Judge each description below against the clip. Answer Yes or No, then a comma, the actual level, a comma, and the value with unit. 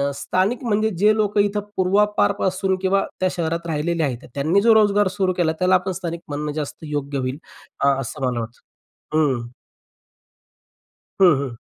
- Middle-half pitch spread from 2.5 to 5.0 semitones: No, wide, 5.4 semitones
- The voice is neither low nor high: Yes, medium, 170 Hz